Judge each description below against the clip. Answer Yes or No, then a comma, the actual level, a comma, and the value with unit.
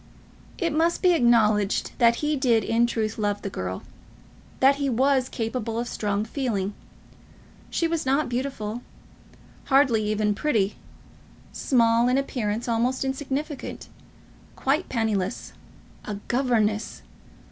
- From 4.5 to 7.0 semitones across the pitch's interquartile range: No, average, 4.1 semitones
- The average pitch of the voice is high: Yes, high, 235 Hz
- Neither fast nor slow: No, slow, 125 wpm